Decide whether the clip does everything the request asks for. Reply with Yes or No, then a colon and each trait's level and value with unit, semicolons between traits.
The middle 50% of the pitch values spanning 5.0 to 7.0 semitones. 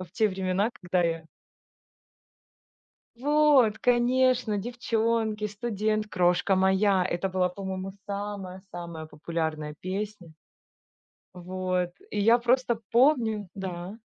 No: average, 3.8 semitones